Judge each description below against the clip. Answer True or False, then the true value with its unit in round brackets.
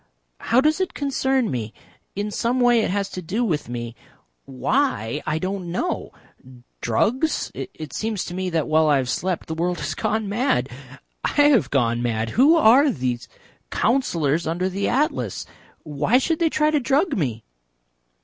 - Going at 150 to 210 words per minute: True (170 wpm)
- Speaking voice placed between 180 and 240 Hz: True (190 Hz)